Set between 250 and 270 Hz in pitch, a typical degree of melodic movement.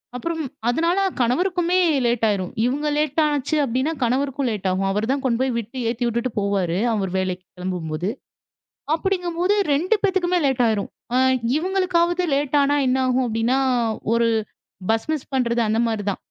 No: very high, 255 Hz; wide, 6.4 semitones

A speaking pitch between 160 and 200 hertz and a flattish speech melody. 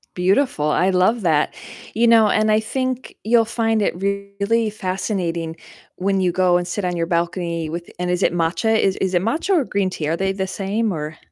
No: high, 190 Hz; average, 3.8 semitones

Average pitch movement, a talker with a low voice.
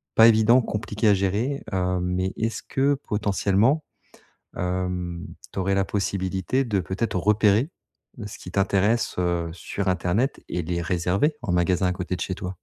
Yes: average, 3.4 semitones; very low, 95 Hz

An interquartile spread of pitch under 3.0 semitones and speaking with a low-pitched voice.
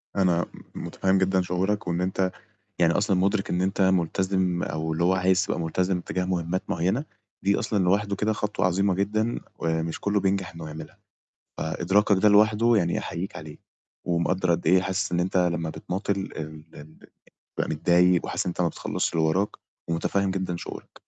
Yes: narrow, 2.4 semitones; very low, 90 Hz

